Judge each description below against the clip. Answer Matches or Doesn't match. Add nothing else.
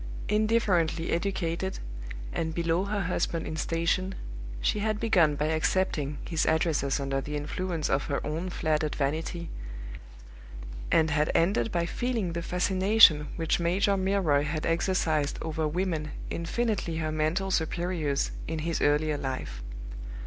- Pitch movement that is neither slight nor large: Matches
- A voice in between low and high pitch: Matches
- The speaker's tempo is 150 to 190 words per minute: Doesn't match